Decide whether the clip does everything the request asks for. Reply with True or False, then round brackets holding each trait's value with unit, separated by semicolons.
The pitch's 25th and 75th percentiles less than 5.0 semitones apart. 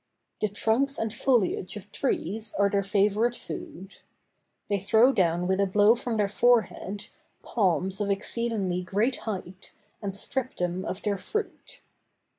True (2.9 semitones)